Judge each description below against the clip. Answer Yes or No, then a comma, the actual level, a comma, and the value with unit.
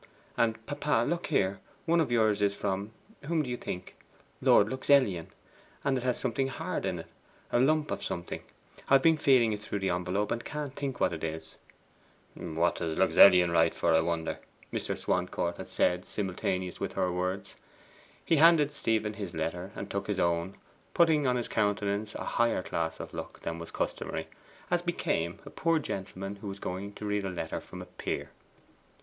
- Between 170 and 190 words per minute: Yes, average, 185 wpm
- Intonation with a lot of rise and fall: Yes, wide, 6.5 semitones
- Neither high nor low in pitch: No, low, 100 Hz